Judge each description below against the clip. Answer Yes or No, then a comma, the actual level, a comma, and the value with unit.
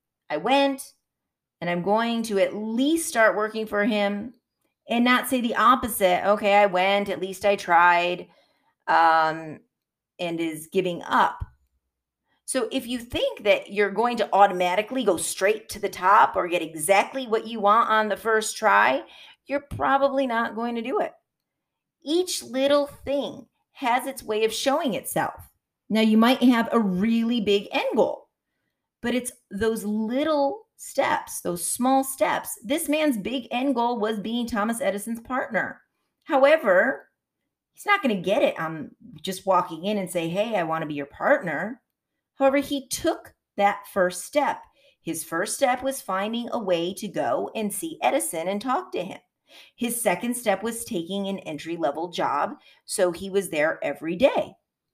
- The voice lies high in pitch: Yes, high, 220 Hz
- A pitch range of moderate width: No, wide, 5.8 semitones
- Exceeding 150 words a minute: Yes, average, 165 wpm